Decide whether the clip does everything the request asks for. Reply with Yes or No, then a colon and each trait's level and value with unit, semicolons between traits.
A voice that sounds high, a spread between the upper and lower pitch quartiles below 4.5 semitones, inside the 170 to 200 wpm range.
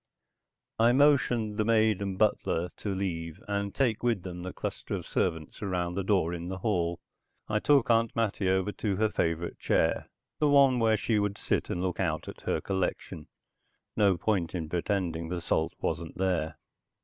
No: very low, 95 Hz; average, 3.9 semitones; average, 180 wpm